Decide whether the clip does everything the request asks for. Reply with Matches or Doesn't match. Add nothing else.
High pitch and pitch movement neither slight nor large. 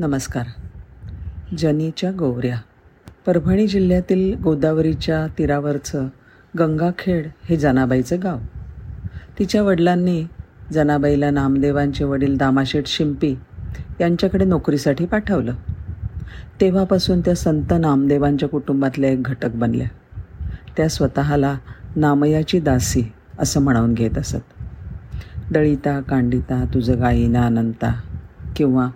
Doesn't match